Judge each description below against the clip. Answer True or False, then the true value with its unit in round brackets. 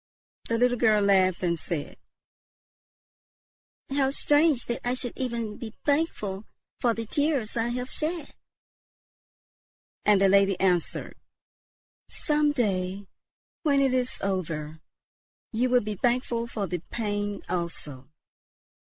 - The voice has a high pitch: True (225 Hz)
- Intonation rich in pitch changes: False (4.8 semitones)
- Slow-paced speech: True (120 wpm)